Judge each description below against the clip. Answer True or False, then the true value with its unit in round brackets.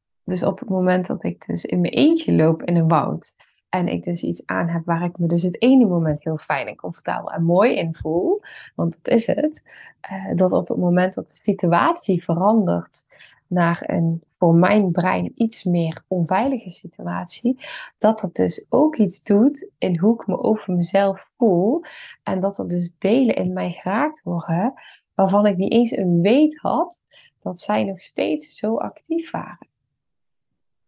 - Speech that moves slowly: False (180 wpm)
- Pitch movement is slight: False (5.0 semitones)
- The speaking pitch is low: False (185 Hz)